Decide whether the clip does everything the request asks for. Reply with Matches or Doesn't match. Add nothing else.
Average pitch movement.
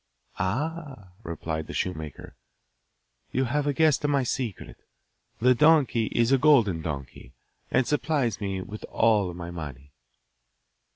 Doesn't match